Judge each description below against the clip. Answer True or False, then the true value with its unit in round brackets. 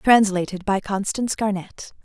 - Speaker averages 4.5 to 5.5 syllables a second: True (4.7 syllables/s)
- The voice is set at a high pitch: True (200 Hz)